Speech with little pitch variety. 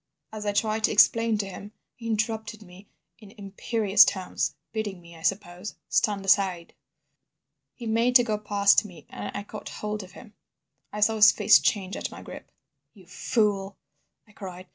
Yes: narrow, 2.0 semitones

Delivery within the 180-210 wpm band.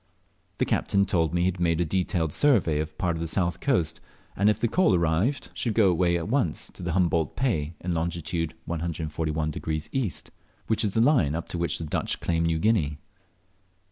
Yes: average, 195 wpm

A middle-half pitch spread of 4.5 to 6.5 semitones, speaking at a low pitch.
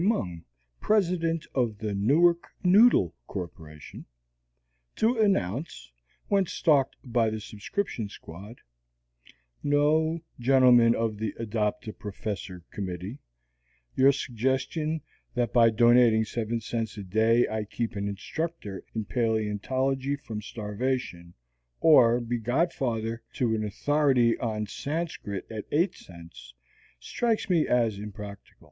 Yes: average, 5.3 semitones; low, 115 Hz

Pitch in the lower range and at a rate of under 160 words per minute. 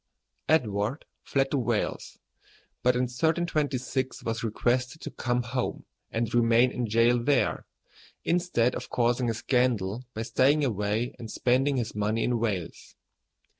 Yes: low, 120 Hz; slow, 135 wpm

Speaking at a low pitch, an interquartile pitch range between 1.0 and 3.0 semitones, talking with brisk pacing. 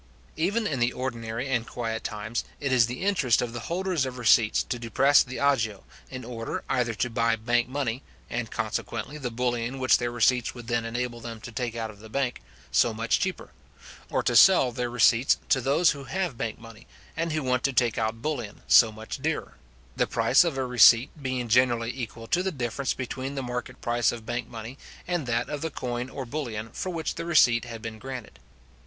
Yes: low, 120 Hz; average, 2.7 semitones; fast, 210 wpm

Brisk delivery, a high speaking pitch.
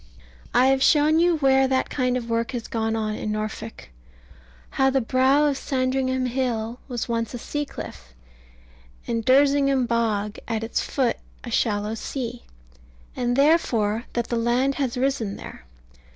No: average, 155 wpm; high, 245 Hz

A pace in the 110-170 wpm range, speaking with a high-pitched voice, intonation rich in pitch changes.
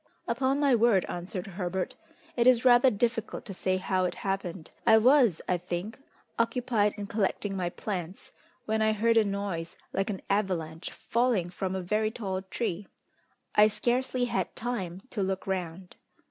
No: average, 160 wpm; high, 200 Hz; average, 3.7 semitones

